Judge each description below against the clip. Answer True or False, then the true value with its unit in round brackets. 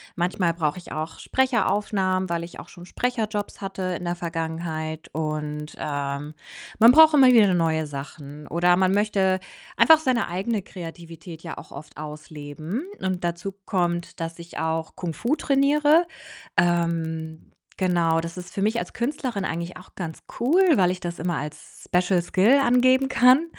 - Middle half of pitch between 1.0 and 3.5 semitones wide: False (4.5 semitones)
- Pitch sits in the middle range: True (175 Hz)